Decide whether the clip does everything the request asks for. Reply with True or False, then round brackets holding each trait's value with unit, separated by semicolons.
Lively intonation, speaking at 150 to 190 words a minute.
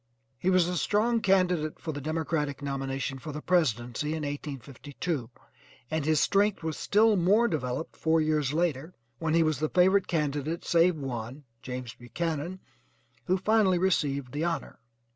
False (4.2 semitones; 155 wpm)